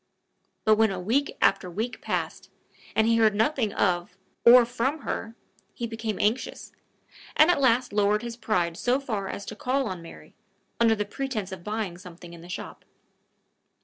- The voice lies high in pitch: Yes, high, 220 Hz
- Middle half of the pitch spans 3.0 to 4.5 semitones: Yes, average, 4.1 semitones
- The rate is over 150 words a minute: Yes, average, 175 wpm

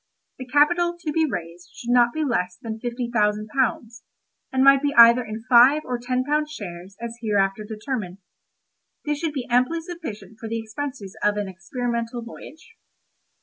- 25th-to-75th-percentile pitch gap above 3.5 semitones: Yes, average, 4.7 semitones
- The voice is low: No, high, 240 Hz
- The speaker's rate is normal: Yes, average, 170 wpm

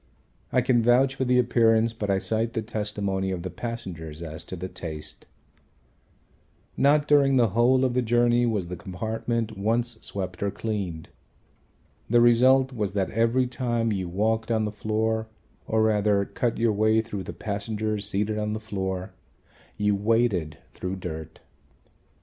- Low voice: Yes, low, 110 Hz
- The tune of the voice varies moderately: Yes, average, 3.4 semitones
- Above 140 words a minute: Yes, average, 160 wpm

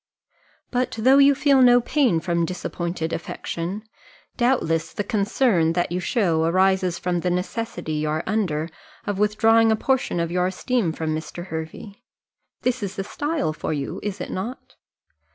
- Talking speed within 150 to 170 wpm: Yes, average, 160 wpm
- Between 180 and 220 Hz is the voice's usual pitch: Yes, high, 190 Hz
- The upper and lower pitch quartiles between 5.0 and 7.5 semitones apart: Yes, wide, 5.5 semitones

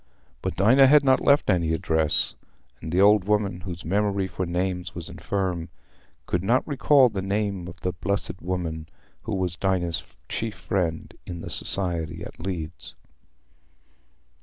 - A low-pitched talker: Yes, very low, 90 Hz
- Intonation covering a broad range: No, average, 2.9 semitones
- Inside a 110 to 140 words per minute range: No, average, 150 wpm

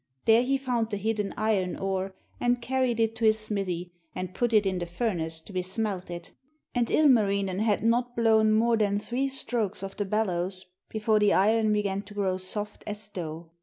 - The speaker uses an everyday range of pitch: Yes, average, 3.2 semitones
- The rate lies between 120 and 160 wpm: No, average, 190 wpm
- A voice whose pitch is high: Yes, high, 210 Hz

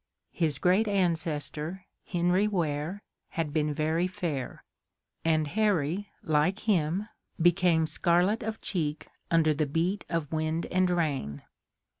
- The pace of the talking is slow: Yes, slow, 120 wpm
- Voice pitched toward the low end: No, medium, 170 Hz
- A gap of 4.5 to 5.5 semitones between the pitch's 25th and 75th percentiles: No, average, 3.2 semitones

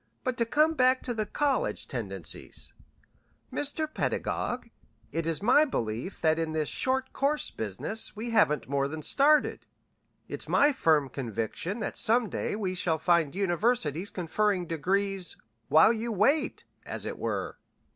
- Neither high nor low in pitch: No, high, 200 Hz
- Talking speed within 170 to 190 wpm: No, average, 145 wpm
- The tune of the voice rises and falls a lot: Yes, wide, 7.9 semitones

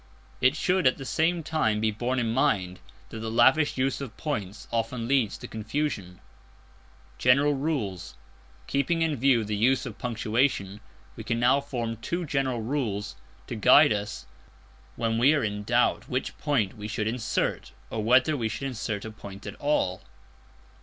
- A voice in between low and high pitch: No, low, 120 Hz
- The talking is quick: No, average, 165 wpm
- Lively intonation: No, average, 4.3 semitones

